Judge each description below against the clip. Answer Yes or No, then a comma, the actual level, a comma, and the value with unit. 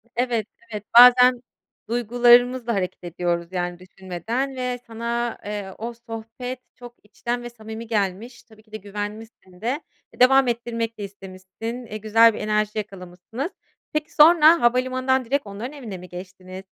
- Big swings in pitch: No, average, 3.6 semitones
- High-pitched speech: Yes, high, 225 Hz